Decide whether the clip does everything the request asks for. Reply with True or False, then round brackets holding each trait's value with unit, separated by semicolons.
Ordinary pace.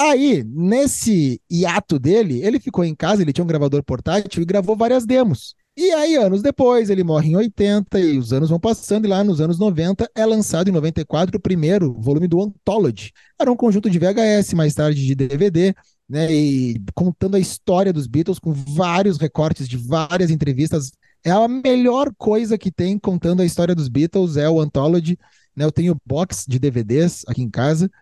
False (190 wpm)